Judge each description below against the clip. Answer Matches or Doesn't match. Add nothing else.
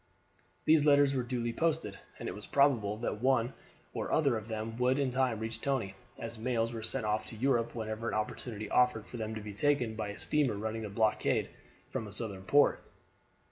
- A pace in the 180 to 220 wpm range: Matches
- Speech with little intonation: Doesn't match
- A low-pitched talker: Matches